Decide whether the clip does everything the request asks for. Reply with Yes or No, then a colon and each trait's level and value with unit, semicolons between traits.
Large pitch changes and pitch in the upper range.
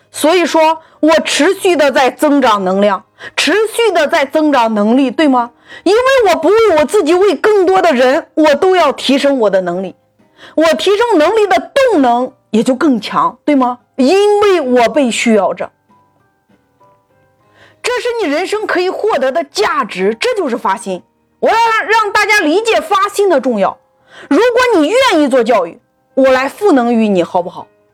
Yes: wide, 8.2 semitones; very high, 305 Hz